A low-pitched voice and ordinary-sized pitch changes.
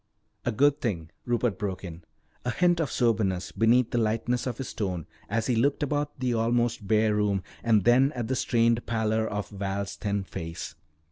Yes: low, 115 Hz; average, 3.3 semitones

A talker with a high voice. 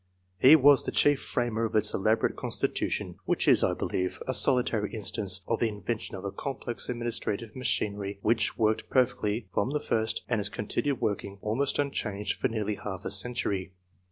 No: low, 110 Hz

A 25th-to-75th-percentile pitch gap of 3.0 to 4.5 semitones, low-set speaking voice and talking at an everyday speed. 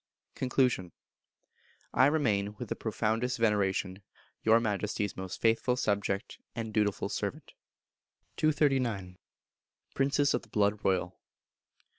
No: average, 3.9 semitones; low, 110 Hz; slow, 105 wpm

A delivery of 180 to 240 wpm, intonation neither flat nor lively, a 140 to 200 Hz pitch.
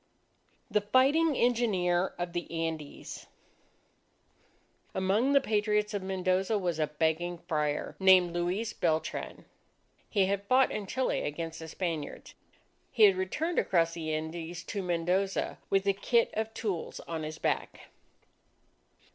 No: slow, 135 wpm; average, 4.0 semitones; medium, 185 Hz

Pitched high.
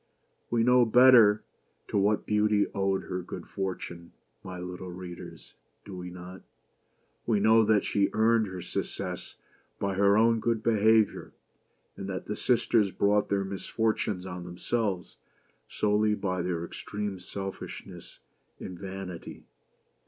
No: low, 100 Hz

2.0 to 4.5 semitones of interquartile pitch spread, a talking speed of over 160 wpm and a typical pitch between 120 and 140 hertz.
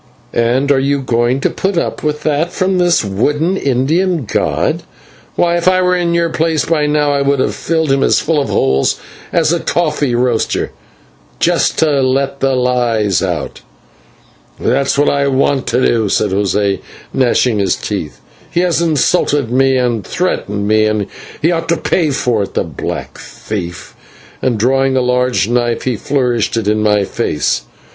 No: average, 5.0 semitones; average, 170 wpm; low, 135 Hz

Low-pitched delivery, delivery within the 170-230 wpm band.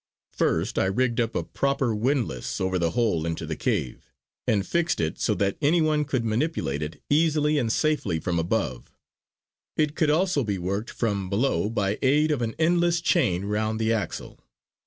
Yes: low, 115 Hz; average, 180 wpm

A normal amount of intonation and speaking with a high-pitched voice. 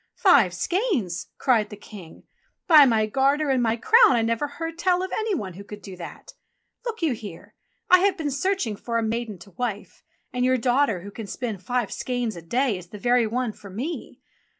No: wide, 5.8 semitones; high, 240 Hz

